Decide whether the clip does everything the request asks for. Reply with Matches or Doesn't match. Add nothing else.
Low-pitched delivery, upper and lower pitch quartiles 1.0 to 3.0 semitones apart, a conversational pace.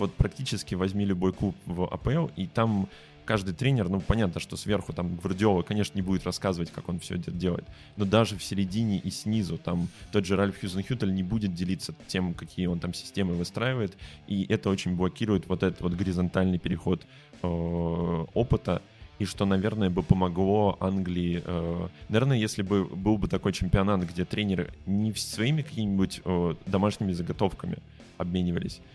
Doesn't match